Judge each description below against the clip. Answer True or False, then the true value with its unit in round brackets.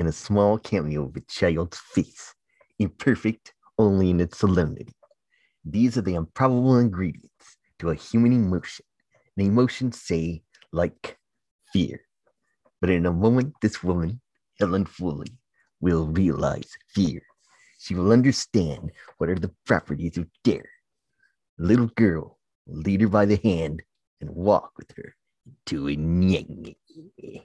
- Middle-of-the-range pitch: False (100 Hz)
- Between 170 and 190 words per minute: False (140 wpm)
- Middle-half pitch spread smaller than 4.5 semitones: False (5.1 semitones)